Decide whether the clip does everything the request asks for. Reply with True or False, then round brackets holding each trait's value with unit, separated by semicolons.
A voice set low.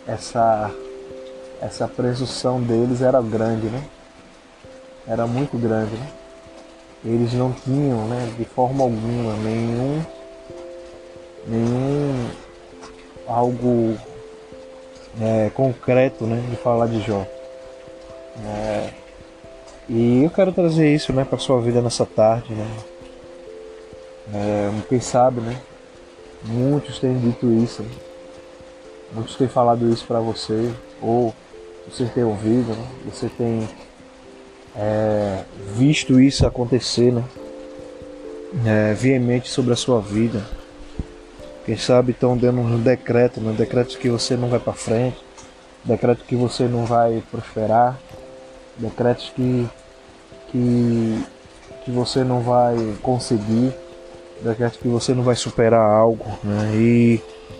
True (115 Hz)